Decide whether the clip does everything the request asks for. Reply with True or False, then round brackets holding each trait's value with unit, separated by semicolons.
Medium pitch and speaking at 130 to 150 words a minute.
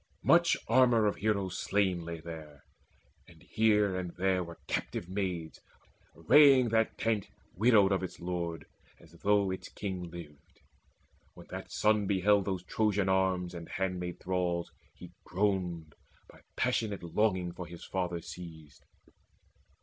False (95 Hz; 135 wpm)